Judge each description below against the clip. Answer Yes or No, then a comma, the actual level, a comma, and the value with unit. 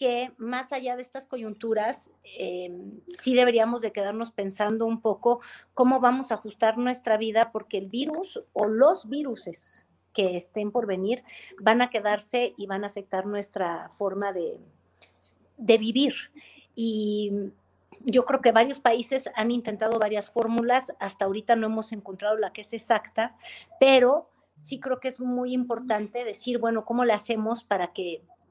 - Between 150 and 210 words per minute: Yes, average, 160 wpm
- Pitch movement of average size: Yes, average, 3.0 semitones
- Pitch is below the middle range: No, high, 230 Hz